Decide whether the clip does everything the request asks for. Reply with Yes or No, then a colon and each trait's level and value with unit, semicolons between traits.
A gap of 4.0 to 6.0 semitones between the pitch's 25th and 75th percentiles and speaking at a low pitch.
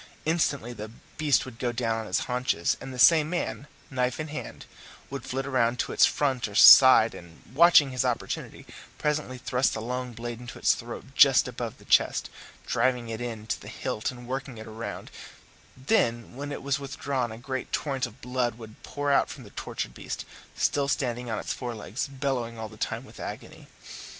No: average, 2.9 semitones; low, 125 Hz